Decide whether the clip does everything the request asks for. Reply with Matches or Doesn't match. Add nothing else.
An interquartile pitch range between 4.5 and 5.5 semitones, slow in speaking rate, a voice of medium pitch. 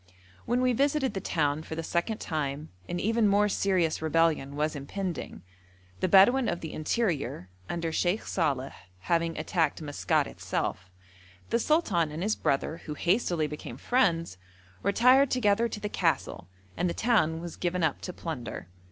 Doesn't match